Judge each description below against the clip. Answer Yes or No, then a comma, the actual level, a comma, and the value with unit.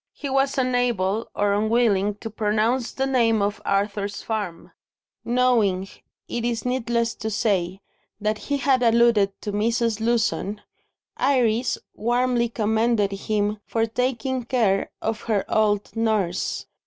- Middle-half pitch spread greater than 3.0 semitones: No, average, 2.7 semitones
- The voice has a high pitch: Yes, high, 225 Hz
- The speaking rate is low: Yes, slow, 130 wpm